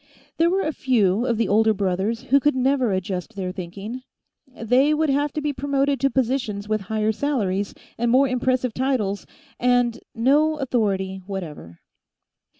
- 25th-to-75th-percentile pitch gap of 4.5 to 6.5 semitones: Yes, average, 5.2 semitones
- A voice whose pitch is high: Yes, high, 240 Hz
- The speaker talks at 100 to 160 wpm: Yes, average, 155 wpm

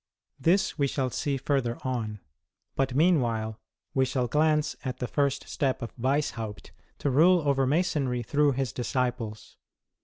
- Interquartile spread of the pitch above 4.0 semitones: No, average, 3.1 semitones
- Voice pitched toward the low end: Yes, low, 130 Hz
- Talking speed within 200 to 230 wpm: No, average, 145 wpm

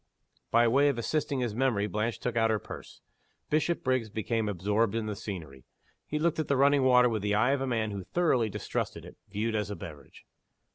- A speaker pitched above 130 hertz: No, low, 115 Hz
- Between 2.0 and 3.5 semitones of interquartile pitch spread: No, average, 4.1 semitones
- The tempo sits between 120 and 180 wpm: No, fast, 205 wpm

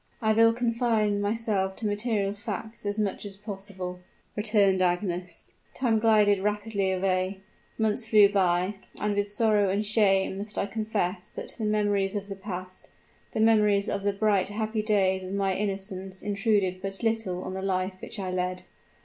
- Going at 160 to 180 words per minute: Yes, average, 165 wpm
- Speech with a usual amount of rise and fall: No, narrow, 2.0 semitones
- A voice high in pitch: Yes, high, 205 Hz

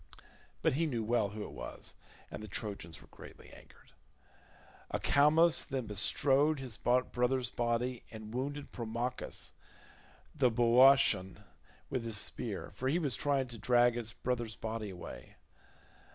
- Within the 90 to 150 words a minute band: Yes, average, 140 wpm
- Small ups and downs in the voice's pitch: No, average, 3.3 semitones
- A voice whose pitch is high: No, low, 120 Hz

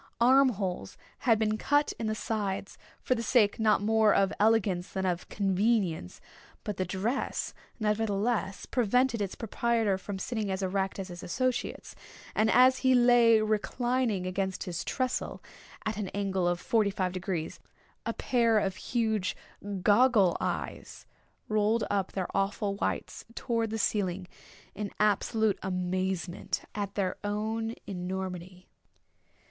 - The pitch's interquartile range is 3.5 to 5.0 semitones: No, average, 3.1 semitones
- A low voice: No, high, 205 Hz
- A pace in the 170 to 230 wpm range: No, average, 140 wpm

